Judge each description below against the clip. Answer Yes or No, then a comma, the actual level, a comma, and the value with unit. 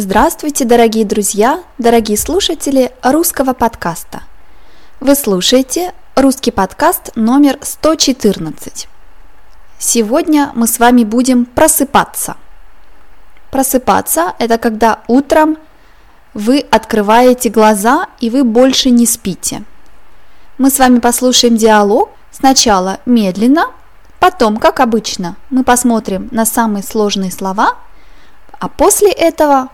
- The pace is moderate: No, slow, 100 wpm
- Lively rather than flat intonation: No, average, 3.9 semitones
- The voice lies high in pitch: Yes, high, 245 Hz